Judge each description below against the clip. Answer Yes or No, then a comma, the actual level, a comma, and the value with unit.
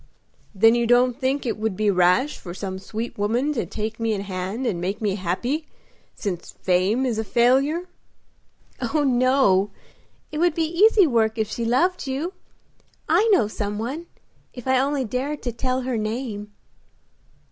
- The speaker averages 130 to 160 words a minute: No, average, 170 wpm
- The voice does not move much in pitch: No, average, 4.6 semitones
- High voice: Yes, high, 235 Hz